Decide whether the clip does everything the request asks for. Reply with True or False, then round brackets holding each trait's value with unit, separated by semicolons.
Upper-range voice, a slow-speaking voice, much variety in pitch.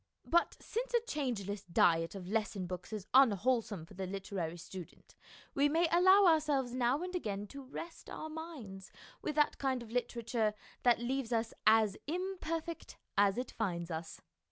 False (235 Hz; 160 wpm; 7.5 semitones)